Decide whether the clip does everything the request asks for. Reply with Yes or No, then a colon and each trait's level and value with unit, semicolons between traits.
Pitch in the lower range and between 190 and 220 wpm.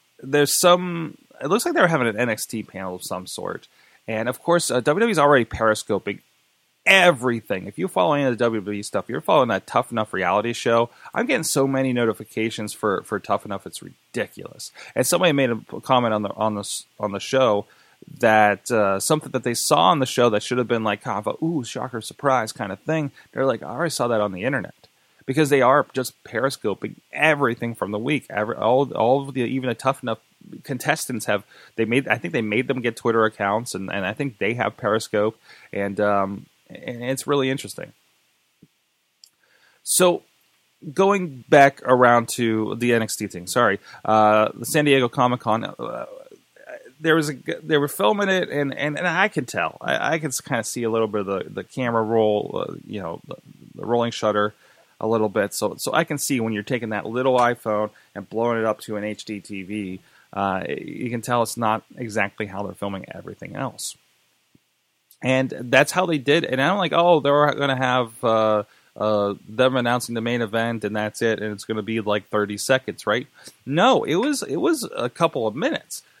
Yes: low, 115 Hz; average, 200 wpm